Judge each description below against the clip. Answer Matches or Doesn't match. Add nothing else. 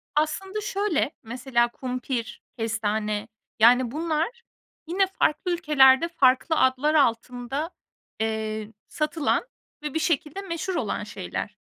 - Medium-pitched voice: Doesn't match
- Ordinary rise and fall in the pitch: Doesn't match